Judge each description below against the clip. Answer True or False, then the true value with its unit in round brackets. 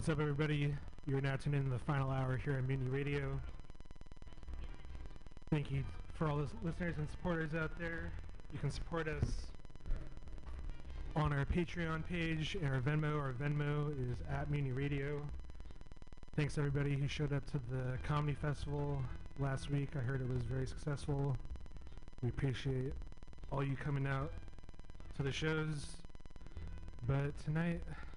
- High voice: False (135 Hz)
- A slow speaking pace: False (150 wpm)